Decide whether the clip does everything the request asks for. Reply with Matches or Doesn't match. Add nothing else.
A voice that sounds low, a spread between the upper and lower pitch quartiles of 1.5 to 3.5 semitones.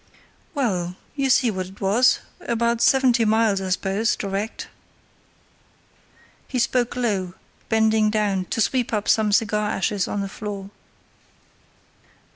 Doesn't match